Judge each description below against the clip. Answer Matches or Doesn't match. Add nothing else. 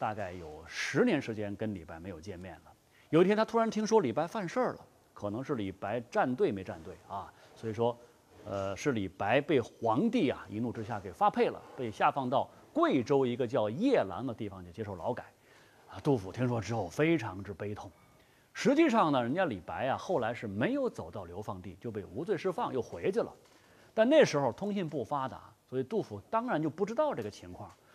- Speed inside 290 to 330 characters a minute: Matches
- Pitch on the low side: Matches